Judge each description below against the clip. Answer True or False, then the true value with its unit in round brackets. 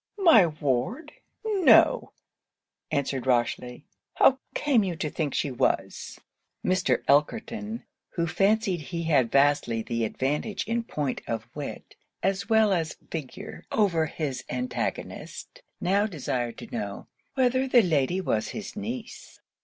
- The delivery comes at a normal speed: False (130 wpm)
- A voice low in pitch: False (165 Hz)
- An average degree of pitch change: False (8.5 semitones)